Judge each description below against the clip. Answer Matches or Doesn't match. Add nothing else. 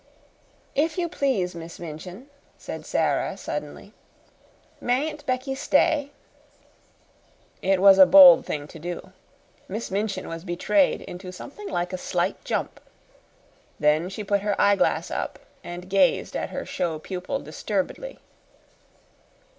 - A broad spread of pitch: Matches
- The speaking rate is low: Matches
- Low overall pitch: Doesn't match